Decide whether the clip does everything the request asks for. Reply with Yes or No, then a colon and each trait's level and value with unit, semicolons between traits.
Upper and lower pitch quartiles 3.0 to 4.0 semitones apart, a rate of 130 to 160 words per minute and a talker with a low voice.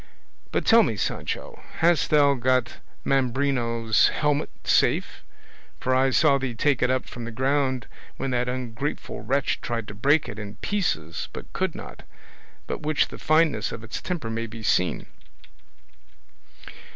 Yes: average, 3.7 semitones; average, 150 wpm; low, 130 Hz